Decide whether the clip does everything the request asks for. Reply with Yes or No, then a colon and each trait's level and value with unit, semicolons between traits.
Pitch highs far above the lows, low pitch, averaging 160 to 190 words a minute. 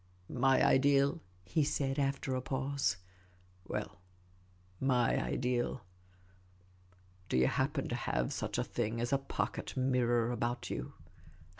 No: wide, 6.6 semitones; low, 120 Hz; average, 145 wpm